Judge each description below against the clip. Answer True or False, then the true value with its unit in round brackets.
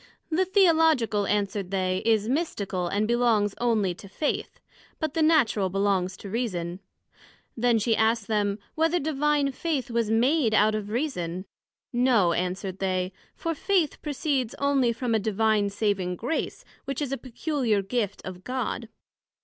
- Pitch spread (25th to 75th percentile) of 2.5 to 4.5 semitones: False (5.6 semitones)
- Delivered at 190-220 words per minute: False (150 wpm)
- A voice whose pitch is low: False (225 Hz)